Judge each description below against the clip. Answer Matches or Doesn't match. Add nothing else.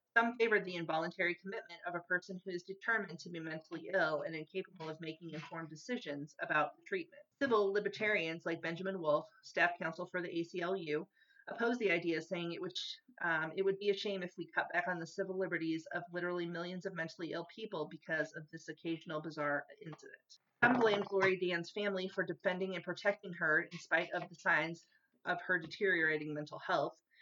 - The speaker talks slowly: Doesn't match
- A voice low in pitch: Doesn't match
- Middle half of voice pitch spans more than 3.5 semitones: Doesn't match